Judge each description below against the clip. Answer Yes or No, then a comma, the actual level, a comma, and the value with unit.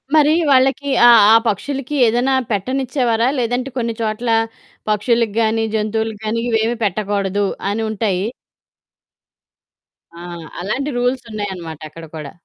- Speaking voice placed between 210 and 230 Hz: Yes, high, 225 Hz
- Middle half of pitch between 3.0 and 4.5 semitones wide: Yes, average, 3.3 semitones